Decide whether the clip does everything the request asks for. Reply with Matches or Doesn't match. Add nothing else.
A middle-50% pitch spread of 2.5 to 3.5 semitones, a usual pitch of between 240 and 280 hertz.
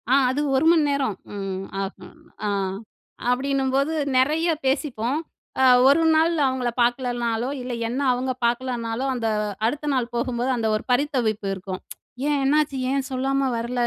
Matches